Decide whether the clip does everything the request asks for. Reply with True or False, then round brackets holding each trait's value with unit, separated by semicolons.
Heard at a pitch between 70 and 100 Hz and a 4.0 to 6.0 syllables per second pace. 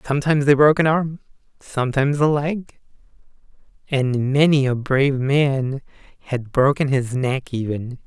False (140 Hz; 4.9 syllables/s)